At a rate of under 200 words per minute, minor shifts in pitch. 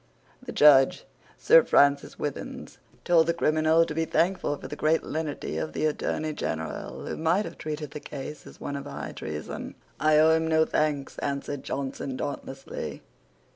Yes: average, 170 wpm; narrow, 2.3 semitones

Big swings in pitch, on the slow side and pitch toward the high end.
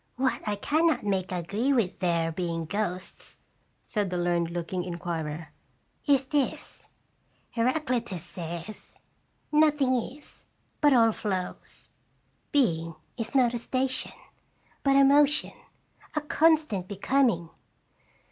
Yes: wide, 7.7 semitones; slow, 120 wpm; high, 215 Hz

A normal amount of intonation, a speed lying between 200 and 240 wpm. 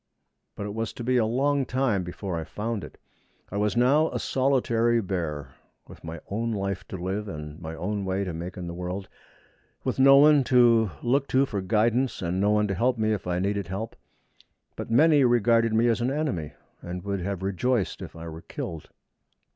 Yes: average, 4.8 semitones; fast, 205 wpm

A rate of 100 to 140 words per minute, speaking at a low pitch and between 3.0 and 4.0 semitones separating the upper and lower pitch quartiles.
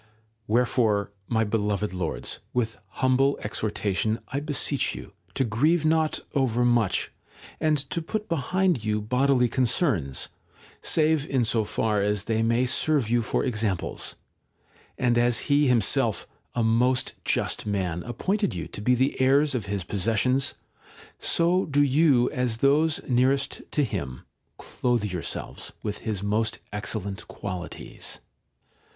No: slow, 135 wpm; low, 120 Hz; average, 4.7 semitones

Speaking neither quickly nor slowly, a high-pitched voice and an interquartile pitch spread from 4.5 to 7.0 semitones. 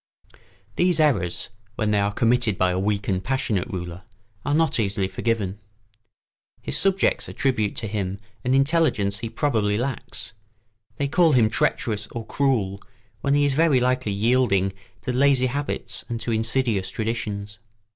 No: average, 155 wpm; low, 115 Hz; average, 4.9 semitones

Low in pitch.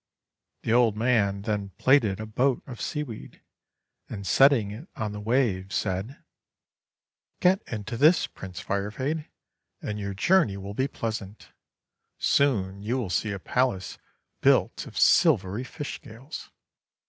Yes: low, 110 Hz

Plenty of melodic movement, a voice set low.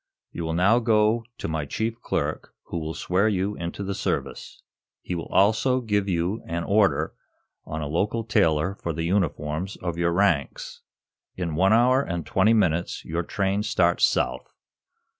No: average, 4.2 semitones; very low, 95 Hz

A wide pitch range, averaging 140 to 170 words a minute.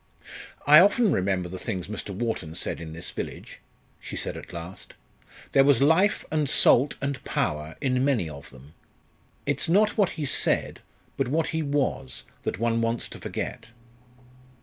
Yes: wide, 8.8 semitones; average, 165 wpm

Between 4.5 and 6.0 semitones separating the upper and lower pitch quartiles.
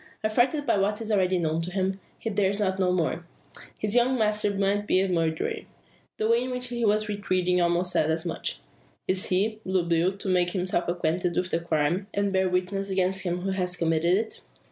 No: average, 2.7 semitones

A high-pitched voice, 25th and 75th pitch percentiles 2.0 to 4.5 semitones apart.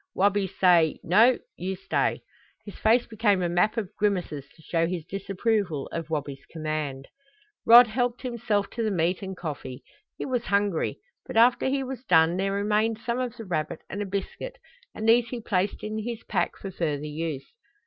No: high, 200 Hz; average, 5.2 semitones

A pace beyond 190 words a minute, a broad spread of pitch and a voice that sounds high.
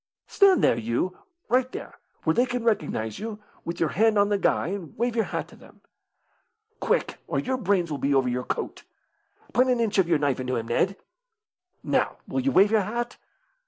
Yes: average, 200 wpm; wide, 8.1 semitones; high, 200 Hz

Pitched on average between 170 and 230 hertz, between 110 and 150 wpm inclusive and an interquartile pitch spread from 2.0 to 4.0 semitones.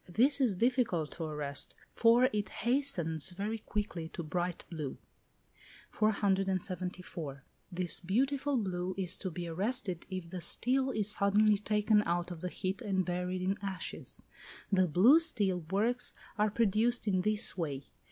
Yes: high, 190 Hz; average, 145 wpm; average, 3.6 semitones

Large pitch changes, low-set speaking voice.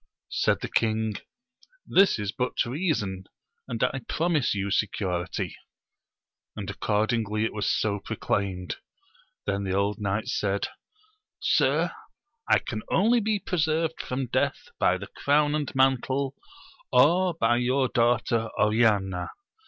Yes: wide, 5.9 semitones; low, 115 Hz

